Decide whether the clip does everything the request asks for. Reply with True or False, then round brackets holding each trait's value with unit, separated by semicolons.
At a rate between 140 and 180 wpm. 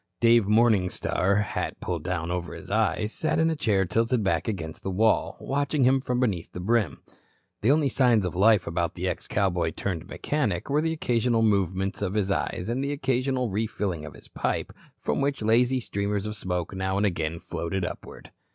False (190 wpm)